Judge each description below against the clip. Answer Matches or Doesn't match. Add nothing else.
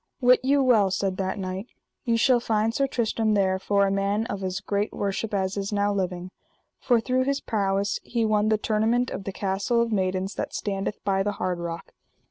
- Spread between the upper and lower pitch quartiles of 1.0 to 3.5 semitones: Matches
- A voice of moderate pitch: Doesn't match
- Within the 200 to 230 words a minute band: Matches